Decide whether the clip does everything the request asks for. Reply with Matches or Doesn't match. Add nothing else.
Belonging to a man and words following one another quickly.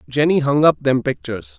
Doesn't match